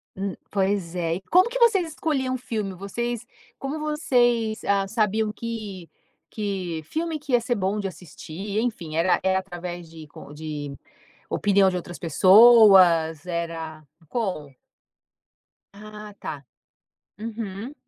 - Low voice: No, high, 200 Hz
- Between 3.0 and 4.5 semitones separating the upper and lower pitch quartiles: No, average, 5.1 semitones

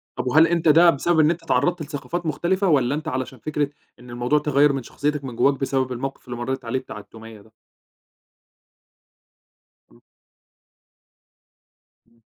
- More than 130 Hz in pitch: Yes, medium, 140 Hz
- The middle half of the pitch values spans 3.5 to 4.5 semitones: Yes, average, 4.0 semitones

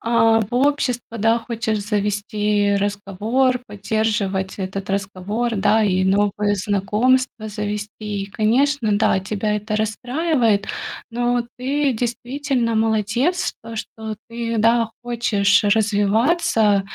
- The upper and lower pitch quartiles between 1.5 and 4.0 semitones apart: Yes, average, 2.7 semitones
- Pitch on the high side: Yes, high, 220 Hz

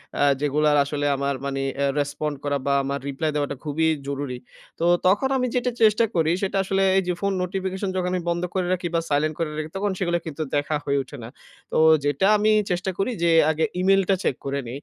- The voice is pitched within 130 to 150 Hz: No, medium, 160 Hz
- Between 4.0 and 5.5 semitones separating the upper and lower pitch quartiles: Yes, average, 4.8 semitones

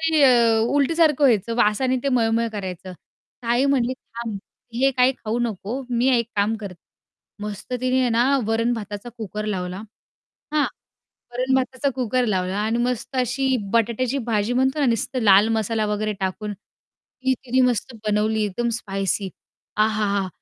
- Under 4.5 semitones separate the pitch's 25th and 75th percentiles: Yes, average, 3.4 semitones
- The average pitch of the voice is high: Yes, high, 230 Hz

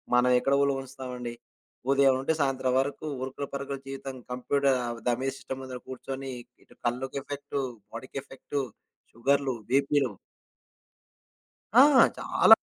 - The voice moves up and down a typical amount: No, narrow, 1.2 semitones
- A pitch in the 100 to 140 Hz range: Yes, low, 135 Hz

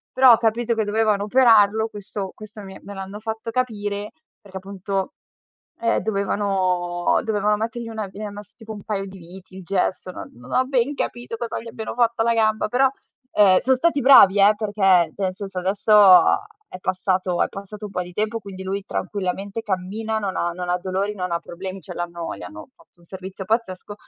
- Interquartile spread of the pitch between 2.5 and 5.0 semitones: Yes, average, 2.8 semitones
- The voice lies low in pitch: No, high, 205 Hz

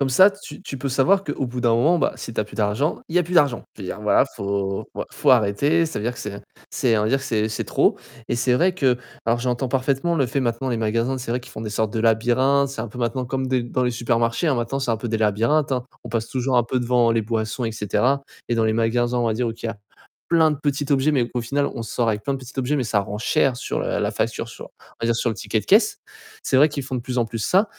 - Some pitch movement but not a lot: Yes, average, 3.2 semitones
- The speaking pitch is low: Yes, low, 120 Hz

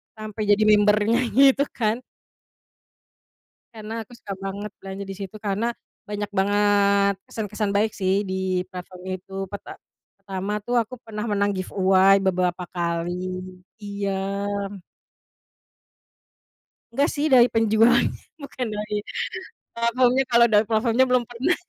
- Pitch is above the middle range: Yes, high, 210 Hz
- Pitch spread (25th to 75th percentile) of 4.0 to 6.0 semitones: No, average, 2.9 semitones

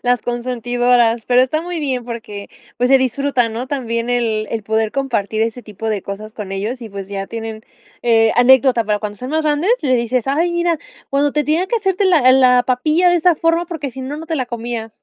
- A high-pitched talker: Yes, high, 245 Hz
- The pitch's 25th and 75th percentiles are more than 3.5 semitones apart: Yes, average, 4.4 semitones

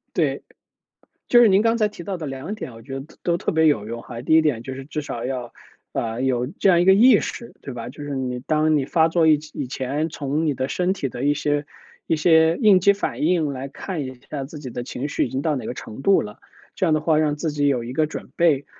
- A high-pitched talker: No, medium, 150 Hz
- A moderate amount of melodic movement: Yes, average, 3.8 semitones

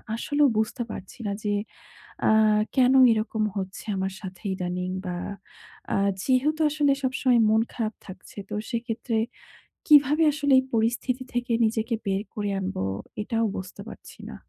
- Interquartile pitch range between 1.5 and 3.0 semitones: No, average, 4.7 semitones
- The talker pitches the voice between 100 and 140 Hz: No, high, 225 Hz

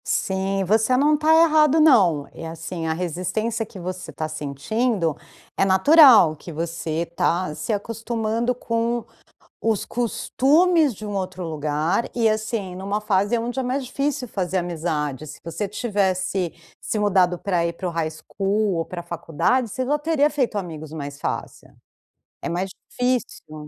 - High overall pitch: Yes, high, 195 Hz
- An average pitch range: No, wide, 5.9 semitones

